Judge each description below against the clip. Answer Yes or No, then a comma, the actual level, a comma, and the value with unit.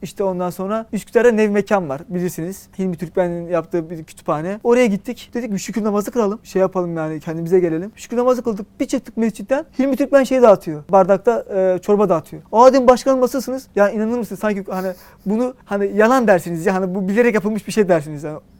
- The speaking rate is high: Yes, fast, 195 wpm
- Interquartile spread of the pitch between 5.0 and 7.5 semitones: No, average, 4.6 semitones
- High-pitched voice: Yes, high, 200 Hz